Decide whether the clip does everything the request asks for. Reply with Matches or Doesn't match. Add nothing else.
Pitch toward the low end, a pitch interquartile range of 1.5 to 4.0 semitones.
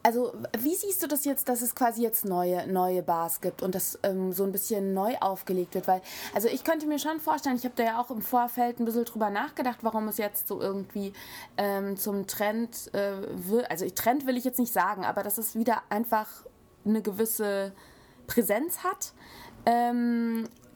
Doesn't match